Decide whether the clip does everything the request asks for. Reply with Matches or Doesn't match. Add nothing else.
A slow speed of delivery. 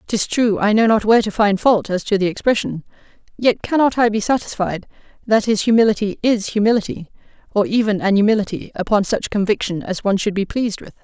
Doesn't match